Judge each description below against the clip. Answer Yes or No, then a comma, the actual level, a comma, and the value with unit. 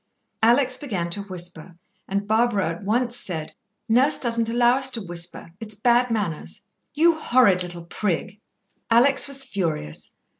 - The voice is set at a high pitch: Yes, high, 215 Hz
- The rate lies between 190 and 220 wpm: No, average, 145 wpm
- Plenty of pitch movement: Yes, wide, 5.7 semitones